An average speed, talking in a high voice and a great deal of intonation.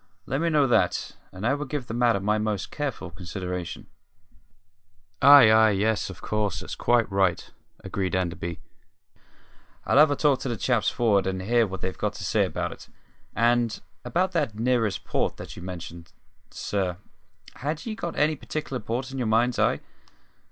No: average, 175 wpm; low, 110 Hz; wide, 5.8 semitones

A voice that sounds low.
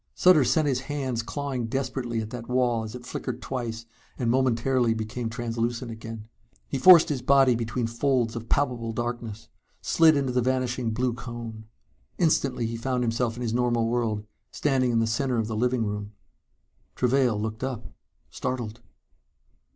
Yes: low, 120 Hz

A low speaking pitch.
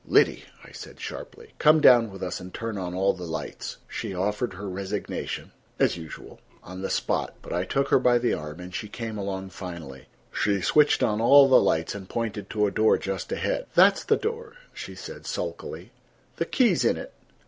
Yes: low, 100 Hz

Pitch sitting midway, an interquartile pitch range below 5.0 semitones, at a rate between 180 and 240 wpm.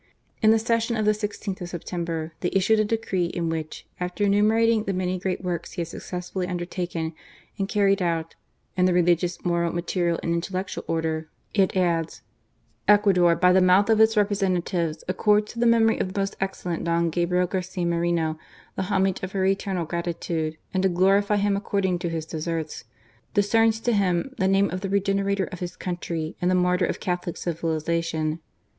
Yes: medium, 180 Hz; average, 2.7 semitones; average, 185 wpm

